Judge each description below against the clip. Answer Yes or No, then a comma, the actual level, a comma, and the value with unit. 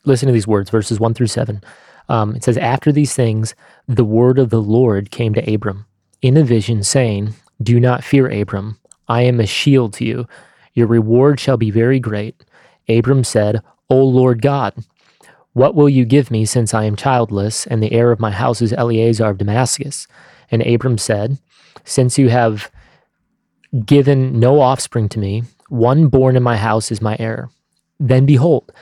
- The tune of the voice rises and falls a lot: No, average, 2.9 semitones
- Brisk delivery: No, average, 180 wpm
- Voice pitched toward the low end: Yes, low, 120 Hz